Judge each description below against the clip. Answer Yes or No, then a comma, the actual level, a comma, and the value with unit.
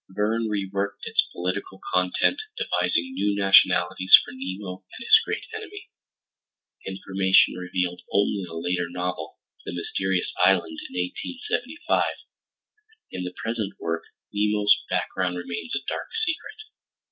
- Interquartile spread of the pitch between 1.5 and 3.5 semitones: Yes, average, 2.8 semitones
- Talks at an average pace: No, slow, 120 wpm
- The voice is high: No, very low, 95 Hz